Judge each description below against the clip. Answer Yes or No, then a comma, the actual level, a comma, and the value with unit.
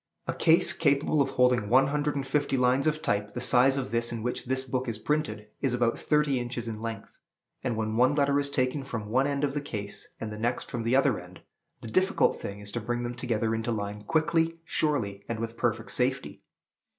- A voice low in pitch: Yes, low, 125 Hz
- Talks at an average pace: No, fast, 225 wpm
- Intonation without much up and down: No, average, 3.8 semitones